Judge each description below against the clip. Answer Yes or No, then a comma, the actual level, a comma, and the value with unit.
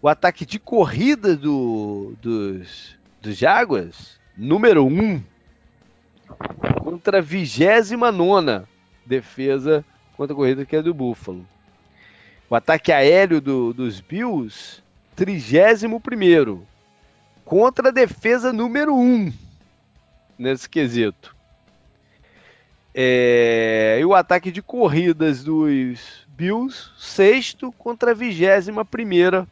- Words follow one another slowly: Yes, slow, 100 wpm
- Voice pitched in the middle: Yes, medium, 160 Hz